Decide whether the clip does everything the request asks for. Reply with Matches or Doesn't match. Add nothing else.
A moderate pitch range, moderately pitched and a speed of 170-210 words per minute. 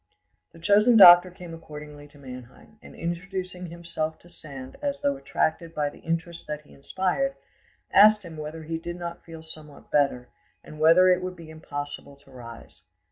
Matches